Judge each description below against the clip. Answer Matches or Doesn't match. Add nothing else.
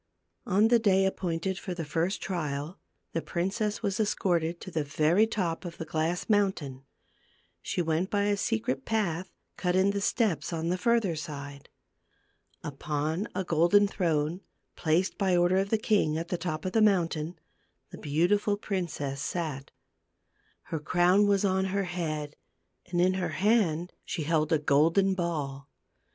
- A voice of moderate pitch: Matches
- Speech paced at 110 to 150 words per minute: Doesn't match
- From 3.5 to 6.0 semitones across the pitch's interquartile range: Matches